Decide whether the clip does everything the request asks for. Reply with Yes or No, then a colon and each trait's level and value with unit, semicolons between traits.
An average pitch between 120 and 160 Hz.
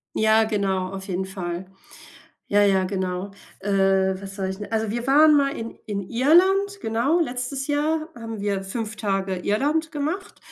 No: high, 215 Hz